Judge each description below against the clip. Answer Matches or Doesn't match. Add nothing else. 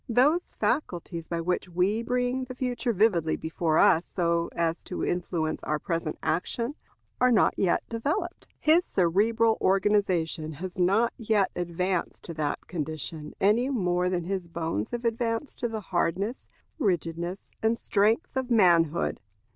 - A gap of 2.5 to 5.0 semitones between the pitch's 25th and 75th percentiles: Doesn't match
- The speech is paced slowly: Doesn't match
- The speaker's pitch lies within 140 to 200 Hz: Matches